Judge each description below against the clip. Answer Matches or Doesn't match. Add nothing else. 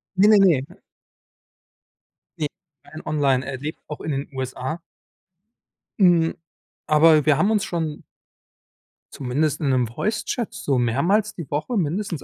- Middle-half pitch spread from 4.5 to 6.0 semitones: Matches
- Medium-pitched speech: Matches